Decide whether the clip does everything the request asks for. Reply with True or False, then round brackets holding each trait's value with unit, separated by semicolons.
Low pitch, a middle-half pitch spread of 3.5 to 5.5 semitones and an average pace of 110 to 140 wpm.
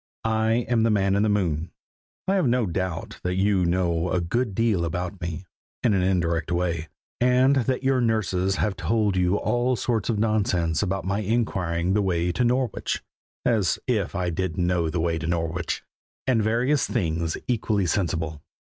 False (95 Hz; 4.7 semitones; 175 wpm)